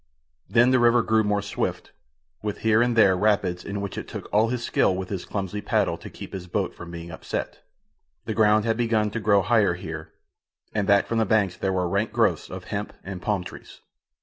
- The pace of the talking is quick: Yes, fast, 215 wpm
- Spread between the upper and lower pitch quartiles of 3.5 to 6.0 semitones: No, average, 2.8 semitones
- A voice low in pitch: Yes, low, 105 Hz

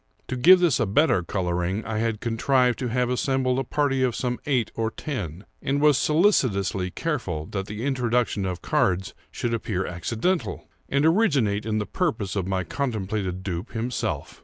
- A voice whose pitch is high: No, low, 115 Hz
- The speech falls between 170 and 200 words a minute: Yes, average, 175 wpm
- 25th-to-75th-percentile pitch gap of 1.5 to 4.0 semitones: No, wide, 5.6 semitones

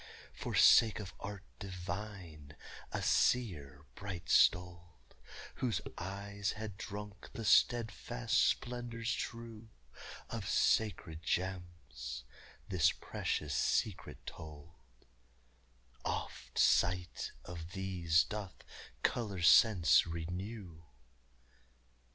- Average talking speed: No, slow, 85 wpm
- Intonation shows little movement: No, average, 4.0 semitones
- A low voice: Yes, very low, 95 Hz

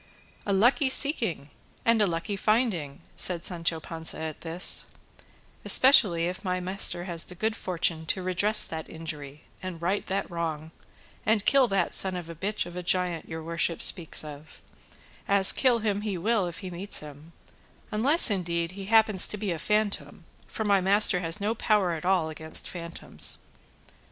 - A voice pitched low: No, medium, 180 Hz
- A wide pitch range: No, average, 3.8 semitones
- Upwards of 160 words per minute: Yes, average, 170 wpm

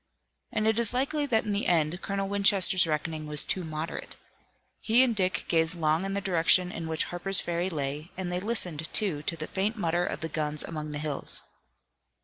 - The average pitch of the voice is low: No, medium, 175 Hz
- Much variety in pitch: No, average, 4.0 semitones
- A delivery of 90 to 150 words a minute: No, average, 200 wpm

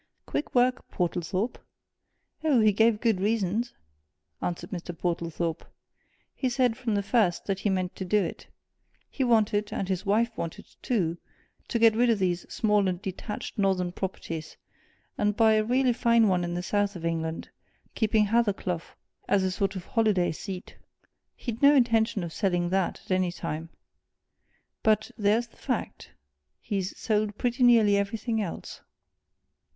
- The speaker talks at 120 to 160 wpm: Yes, average, 155 wpm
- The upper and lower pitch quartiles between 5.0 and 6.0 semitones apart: No, average, 3.9 semitones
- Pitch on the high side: Yes, high, 205 Hz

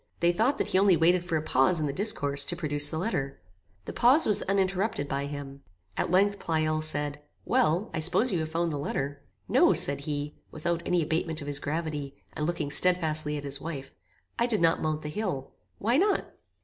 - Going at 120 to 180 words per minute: No, fast, 205 wpm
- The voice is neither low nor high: Yes, medium, 160 Hz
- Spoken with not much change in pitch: No, average, 3.8 semitones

